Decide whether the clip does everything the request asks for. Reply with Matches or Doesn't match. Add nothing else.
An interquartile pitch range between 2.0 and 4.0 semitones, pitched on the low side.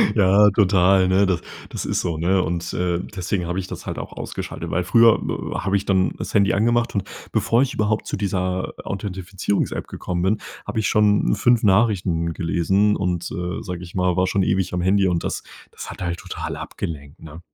Matches